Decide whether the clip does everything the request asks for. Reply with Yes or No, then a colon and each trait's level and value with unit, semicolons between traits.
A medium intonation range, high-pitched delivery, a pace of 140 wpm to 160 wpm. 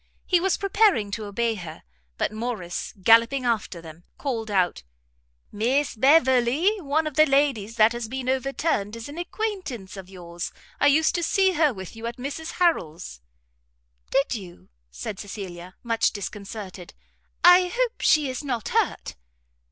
No: wide, 7.0 semitones; high, 235 Hz; average, 150 wpm